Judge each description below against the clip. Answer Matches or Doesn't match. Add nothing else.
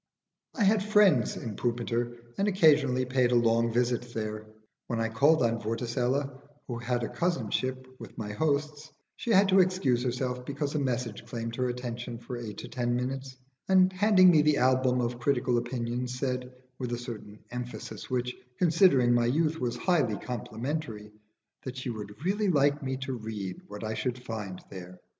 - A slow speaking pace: Doesn't match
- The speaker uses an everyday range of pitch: Matches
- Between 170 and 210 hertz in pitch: Doesn't match